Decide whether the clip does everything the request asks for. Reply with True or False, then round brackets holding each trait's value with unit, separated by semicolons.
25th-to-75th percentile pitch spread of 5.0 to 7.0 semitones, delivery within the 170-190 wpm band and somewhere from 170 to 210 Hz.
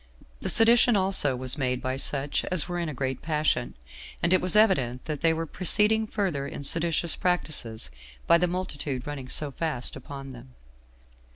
False (5.3 semitones; 175 wpm; 155 Hz)